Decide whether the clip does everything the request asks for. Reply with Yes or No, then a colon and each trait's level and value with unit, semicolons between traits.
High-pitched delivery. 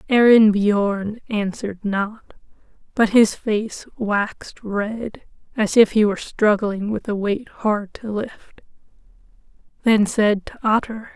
Yes: high, 210 Hz